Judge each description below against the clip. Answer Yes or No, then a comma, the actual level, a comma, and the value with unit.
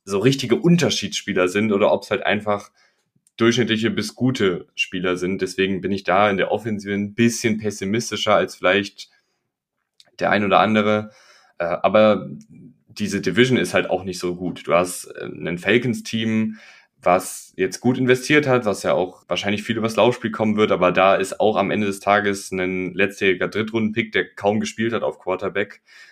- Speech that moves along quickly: No, average, 170 wpm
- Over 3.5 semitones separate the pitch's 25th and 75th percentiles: No, narrow, 2.6 semitones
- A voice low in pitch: Yes, low, 105 Hz